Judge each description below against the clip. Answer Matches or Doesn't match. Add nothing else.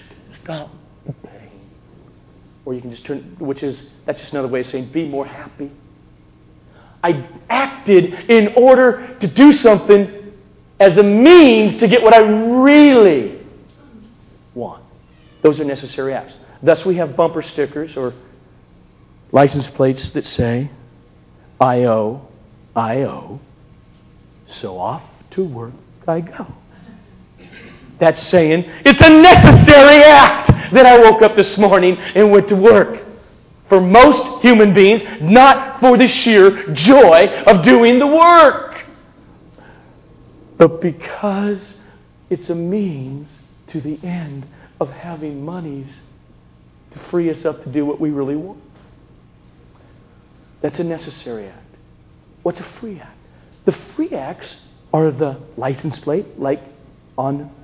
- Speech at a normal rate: Doesn't match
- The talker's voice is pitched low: Doesn't match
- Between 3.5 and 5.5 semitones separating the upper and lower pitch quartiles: Doesn't match